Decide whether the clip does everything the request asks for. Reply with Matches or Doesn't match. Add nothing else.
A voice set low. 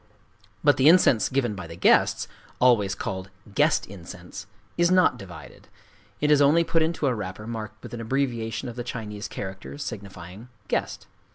Matches